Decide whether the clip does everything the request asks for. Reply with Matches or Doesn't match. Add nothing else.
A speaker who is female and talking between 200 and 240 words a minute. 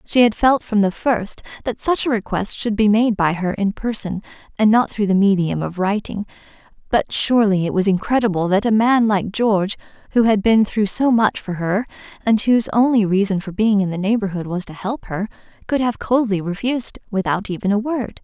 Matches